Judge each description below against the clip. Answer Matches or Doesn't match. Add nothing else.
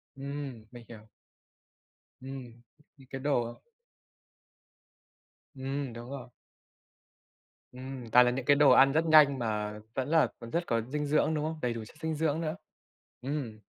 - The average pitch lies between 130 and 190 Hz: Matches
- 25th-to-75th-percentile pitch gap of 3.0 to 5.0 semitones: Matches